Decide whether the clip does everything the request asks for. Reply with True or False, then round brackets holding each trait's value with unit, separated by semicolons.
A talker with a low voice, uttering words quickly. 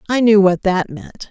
False (190 Hz; 230 wpm)